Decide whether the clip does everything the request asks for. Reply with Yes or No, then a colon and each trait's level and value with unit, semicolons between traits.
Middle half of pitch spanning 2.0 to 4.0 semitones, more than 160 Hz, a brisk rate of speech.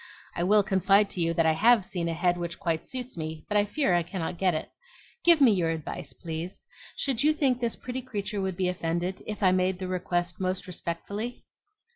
Yes: average, 3.7 semitones; medium, 185 Hz; fast, 215 wpm